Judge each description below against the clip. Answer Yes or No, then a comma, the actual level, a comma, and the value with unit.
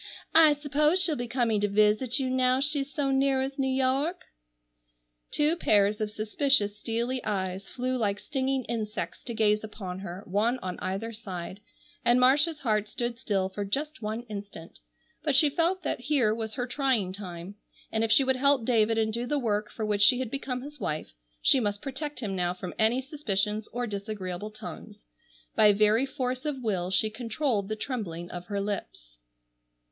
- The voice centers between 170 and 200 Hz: No, high, 225 Hz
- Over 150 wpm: Yes, average, 180 wpm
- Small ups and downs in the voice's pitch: No, average, 4.4 semitones